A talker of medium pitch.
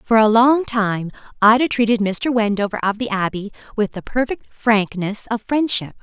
No: high, 220 Hz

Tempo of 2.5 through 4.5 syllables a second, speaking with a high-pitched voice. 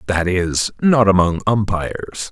No: 4.1 syllables/s; very low, 95 Hz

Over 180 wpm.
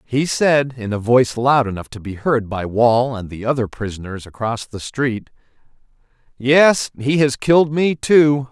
No: average, 175 wpm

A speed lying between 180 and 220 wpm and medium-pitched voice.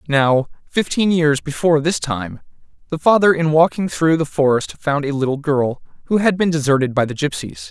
Yes: average, 185 wpm; medium, 150 Hz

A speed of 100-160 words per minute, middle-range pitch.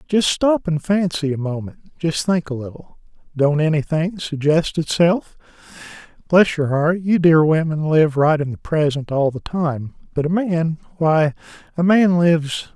Yes: average, 150 wpm; medium, 160 Hz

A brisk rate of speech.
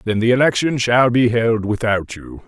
No: average, 195 wpm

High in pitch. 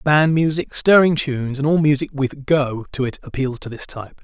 No: medium, 140 Hz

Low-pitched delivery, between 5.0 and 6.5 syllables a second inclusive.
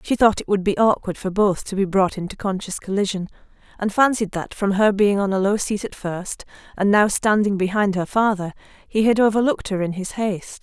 No: high, 200 Hz; 5.5 syllables/s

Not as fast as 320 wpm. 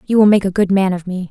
No: fast, 365 wpm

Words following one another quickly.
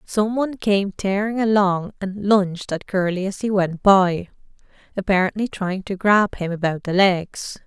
No: average, 165 wpm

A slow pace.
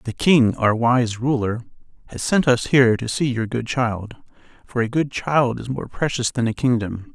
No: average, 200 wpm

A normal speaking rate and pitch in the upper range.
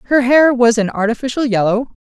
Yes: average, 170 wpm; high, 240 Hz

